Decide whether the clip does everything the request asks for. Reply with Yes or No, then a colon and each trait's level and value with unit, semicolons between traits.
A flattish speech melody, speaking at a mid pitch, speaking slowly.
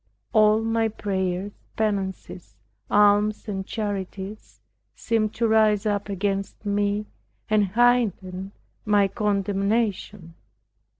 No: narrow, 1.7 semitones; high, 205 Hz; slow, 95 wpm